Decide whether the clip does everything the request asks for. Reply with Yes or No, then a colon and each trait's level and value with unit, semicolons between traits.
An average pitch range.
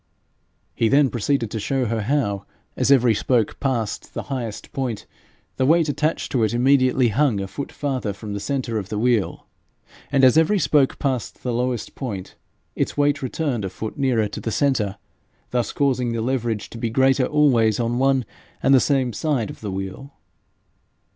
Yes: average, 3.6 semitones